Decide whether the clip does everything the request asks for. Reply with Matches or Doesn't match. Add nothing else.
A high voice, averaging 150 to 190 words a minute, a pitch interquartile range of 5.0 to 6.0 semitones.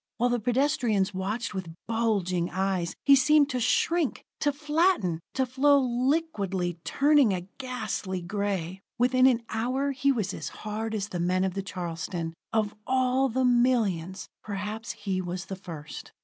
Matches